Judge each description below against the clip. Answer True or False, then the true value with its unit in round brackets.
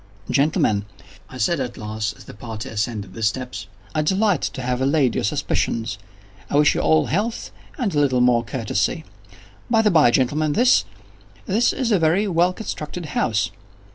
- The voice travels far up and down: True (7.6 semitones)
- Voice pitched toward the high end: False (135 Hz)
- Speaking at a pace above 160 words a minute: True (170 wpm)